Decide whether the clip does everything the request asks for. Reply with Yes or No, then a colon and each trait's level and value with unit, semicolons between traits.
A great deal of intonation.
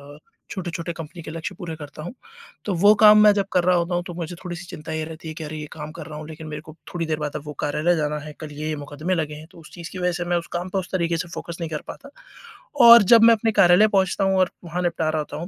No: average, 2.7 semitones